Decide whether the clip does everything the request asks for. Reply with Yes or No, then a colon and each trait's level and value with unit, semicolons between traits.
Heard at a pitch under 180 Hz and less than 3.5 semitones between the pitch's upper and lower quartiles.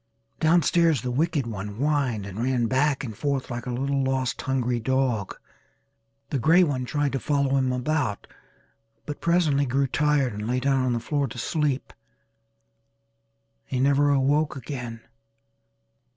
Yes: low, 135 Hz; average, 2.8 semitones